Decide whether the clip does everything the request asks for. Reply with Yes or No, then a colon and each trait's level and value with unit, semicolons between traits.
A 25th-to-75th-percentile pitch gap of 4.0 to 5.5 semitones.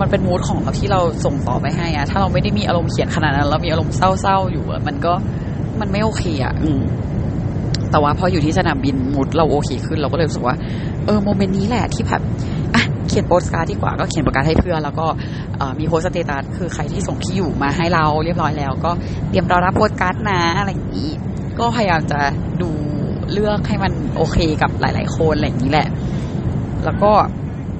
No: narrow, 2.5 semitones